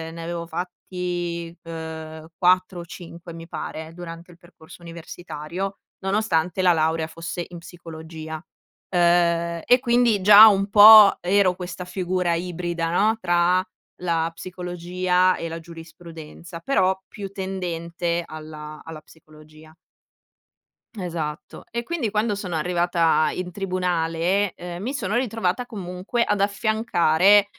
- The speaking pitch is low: No, medium, 175 Hz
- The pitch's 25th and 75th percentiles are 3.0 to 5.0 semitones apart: No, narrow, 2.5 semitones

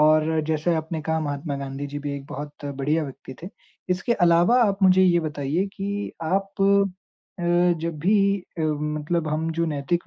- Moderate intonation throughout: Yes, average, 3.0 semitones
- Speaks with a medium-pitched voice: Yes, medium, 155 Hz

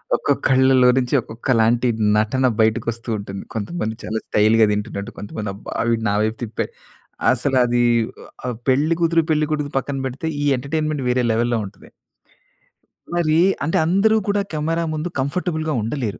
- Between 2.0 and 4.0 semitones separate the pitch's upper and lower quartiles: No, wide, 5.5 semitones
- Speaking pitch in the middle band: No, low, 130 Hz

